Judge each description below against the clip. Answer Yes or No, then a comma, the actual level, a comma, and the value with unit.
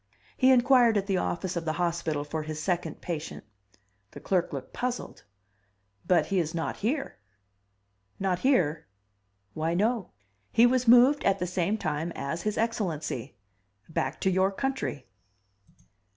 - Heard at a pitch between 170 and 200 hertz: Yes, medium, 185 Hz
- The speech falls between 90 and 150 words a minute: Yes, average, 145 wpm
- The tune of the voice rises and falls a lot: Yes, wide, 6.1 semitones